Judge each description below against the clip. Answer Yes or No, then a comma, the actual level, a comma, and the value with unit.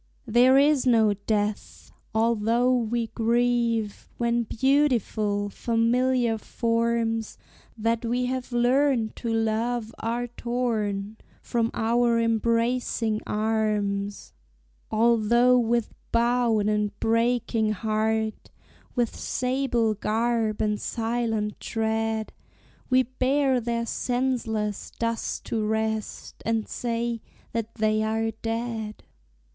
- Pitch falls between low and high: No, high, 230 Hz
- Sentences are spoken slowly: Yes, slow, 95 wpm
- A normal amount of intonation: No, narrow, 1.6 semitones